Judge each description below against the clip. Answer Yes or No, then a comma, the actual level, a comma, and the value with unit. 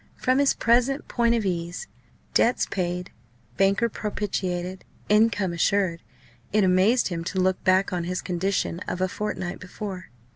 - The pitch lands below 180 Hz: No, high, 190 Hz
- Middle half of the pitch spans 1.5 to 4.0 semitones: Yes, average, 2.9 semitones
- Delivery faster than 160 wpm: No, average, 145 wpm